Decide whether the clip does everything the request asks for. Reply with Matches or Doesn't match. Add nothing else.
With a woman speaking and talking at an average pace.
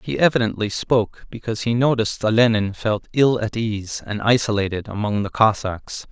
Doesn't match